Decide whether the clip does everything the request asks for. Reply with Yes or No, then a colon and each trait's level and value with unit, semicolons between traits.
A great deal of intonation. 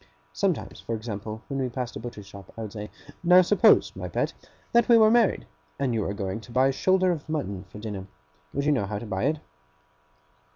Yes: wide, 7.1 semitones